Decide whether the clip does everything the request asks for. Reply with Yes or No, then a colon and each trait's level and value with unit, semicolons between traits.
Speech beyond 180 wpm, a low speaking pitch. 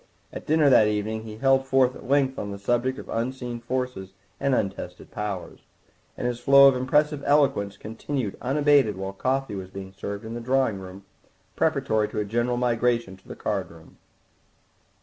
No: average, 175 wpm; low, 120 Hz